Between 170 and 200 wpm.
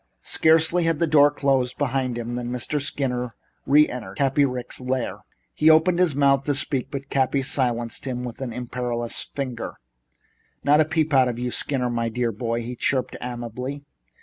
Yes: average, 175 wpm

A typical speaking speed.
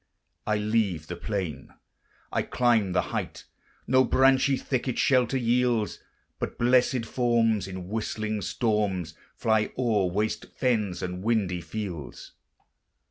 No: slow, 120 wpm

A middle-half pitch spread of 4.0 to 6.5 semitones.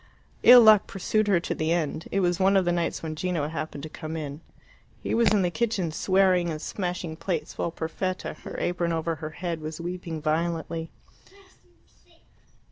No: average, 2.7 semitones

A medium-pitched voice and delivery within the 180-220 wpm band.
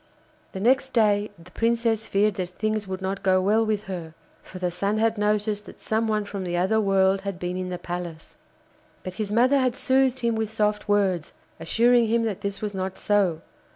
No: high, 205 Hz; fast, 205 wpm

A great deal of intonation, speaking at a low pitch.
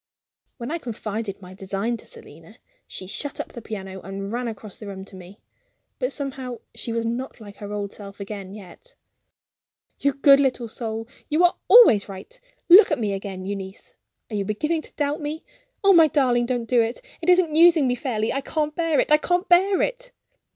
No: wide, 7.1 semitones; high, 240 Hz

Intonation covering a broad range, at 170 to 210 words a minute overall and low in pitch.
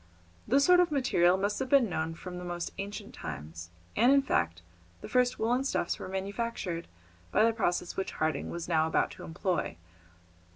No: wide, 6.5 semitones; average, 180 wpm; high, 190 Hz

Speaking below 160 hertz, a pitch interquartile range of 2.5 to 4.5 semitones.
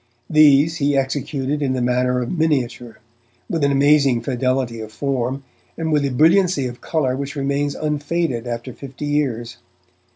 Yes: medium, 140 Hz; average, 2.9 semitones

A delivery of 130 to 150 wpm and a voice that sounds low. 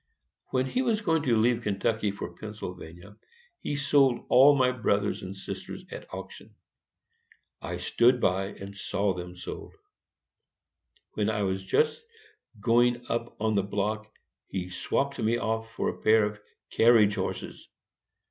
Yes: average, 145 wpm; low, 110 Hz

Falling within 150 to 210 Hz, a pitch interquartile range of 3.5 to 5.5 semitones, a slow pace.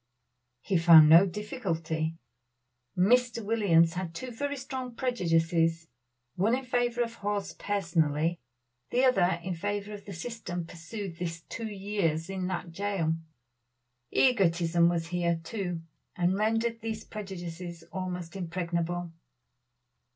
Yes: medium, 185 Hz; average, 4.3 semitones; slow, 120 wpm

